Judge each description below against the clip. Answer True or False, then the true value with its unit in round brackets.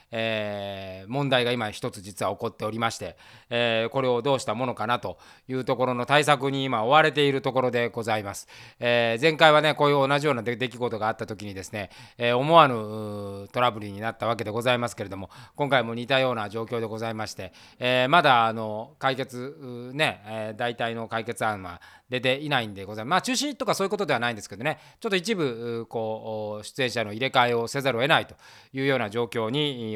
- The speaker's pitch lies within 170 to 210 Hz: False (120 Hz)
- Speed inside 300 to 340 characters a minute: False (435 characters per minute)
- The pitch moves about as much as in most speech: True (3.6 semitones)